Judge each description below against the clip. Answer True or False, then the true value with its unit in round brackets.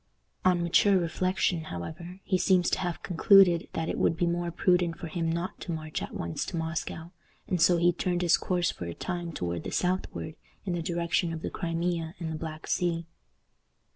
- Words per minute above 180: True (200 wpm)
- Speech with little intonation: True (1.6 semitones)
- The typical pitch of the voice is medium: True (170 Hz)